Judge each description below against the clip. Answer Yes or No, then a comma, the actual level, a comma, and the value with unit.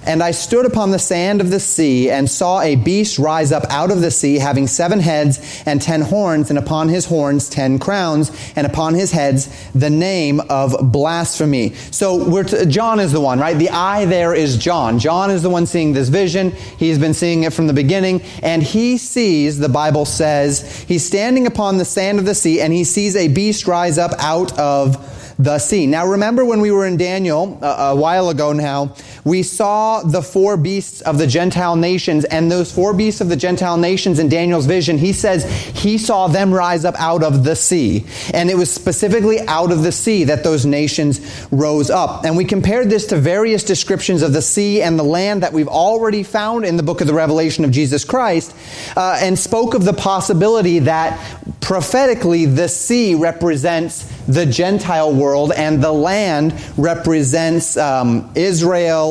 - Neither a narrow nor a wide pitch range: Yes, average, 4.3 semitones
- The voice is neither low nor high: Yes, medium, 165 Hz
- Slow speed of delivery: No, average, 195 wpm